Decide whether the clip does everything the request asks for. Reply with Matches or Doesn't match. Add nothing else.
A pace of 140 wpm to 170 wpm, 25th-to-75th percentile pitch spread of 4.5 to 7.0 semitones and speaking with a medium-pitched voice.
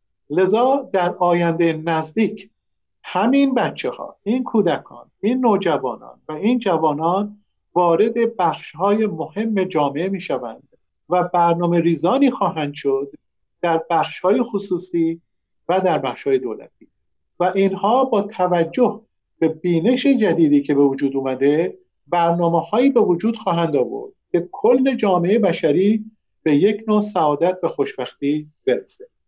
Doesn't match